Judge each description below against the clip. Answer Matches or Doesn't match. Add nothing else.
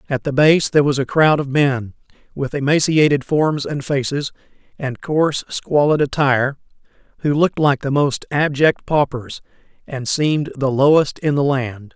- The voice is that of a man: Matches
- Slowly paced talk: Doesn't match